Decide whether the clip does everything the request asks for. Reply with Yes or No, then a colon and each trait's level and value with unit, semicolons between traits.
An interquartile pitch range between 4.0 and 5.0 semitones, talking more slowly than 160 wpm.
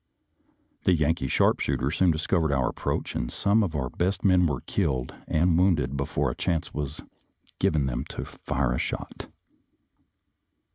Yes: average, 4.7 semitones; average, 150 wpm